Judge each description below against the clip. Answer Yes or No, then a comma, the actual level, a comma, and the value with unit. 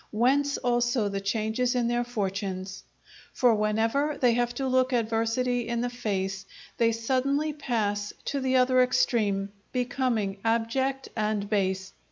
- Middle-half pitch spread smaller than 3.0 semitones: No, average, 3.3 semitones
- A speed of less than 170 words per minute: Yes, average, 140 wpm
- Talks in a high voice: Yes, high, 235 Hz